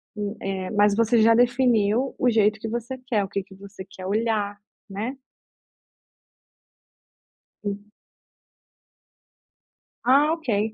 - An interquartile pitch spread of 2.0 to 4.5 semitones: Yes, average, 2.9 semitones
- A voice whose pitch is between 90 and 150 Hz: No, high, 215 Hz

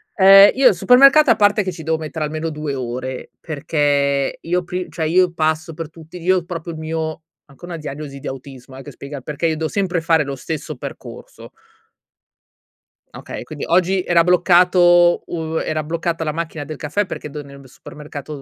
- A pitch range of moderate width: Yes, average, 3.1 semitones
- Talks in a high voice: No, medium, 160 Hz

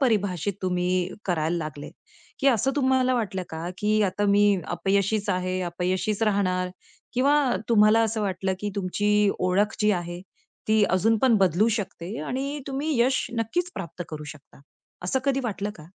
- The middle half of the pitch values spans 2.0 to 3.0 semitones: No, average, 3.7 semitones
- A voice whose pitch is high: Yes, high, 200 Hz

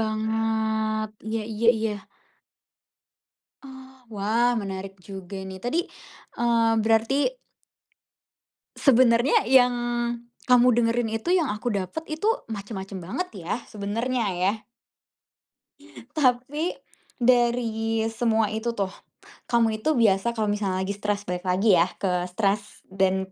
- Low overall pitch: No, high, 220 Hz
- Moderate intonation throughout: Yes, average, 3.2 semitones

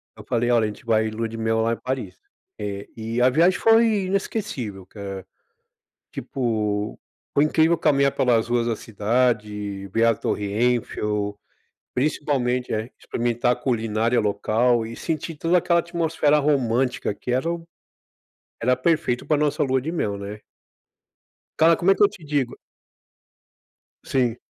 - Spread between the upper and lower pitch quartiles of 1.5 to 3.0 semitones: No, wide, 5.4 semitones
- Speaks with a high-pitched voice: No, low, 120 Hz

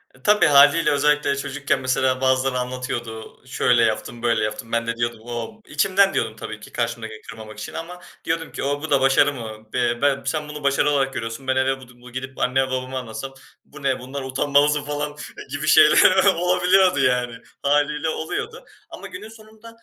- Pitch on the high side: No, low, 135 Hz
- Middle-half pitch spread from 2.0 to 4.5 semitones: Yes, average, 3.4 semitones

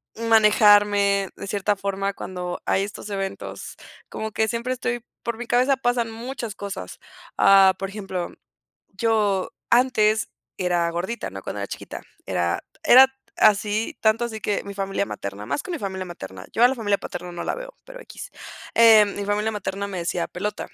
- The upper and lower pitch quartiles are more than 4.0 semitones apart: No, average, 3.0 semitones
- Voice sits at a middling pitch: No, high, 205 Hz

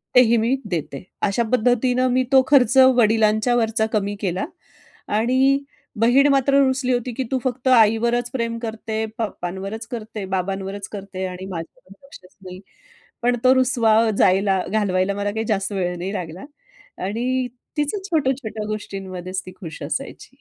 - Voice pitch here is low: No, high, 220 Hz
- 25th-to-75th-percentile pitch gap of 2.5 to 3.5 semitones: No, average, 4.3 semitones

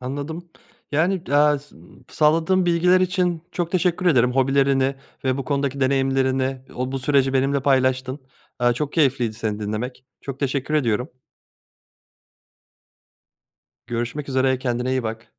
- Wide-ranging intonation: No, average, 2.7 semitones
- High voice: No, low, 135 Hz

